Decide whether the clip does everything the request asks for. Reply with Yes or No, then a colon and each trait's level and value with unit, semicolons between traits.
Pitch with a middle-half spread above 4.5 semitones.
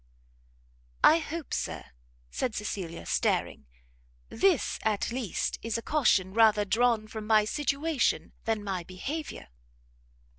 Yes: average, 5.1 semitones